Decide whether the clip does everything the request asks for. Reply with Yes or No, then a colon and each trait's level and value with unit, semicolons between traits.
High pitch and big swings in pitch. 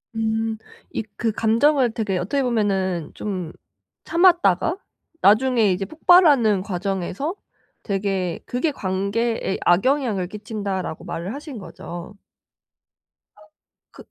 No: high, 210 Hz; average, 4.8 semitones